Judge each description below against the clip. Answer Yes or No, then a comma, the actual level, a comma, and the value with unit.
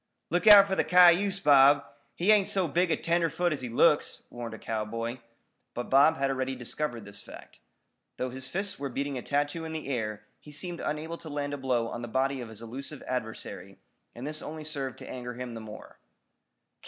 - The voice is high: No, medium, 140 Hz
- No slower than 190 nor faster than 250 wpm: Yes, fast, 205 wpm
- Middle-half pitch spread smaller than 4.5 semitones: No, average, 4.8 semitones